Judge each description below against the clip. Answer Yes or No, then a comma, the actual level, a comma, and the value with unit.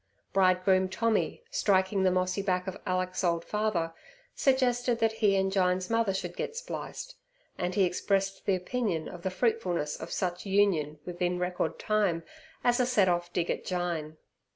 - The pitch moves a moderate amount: Yes, average, 3.0 semitones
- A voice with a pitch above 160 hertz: Yes, medium, 185 Hz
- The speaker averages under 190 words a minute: Yes, average, 165 wpm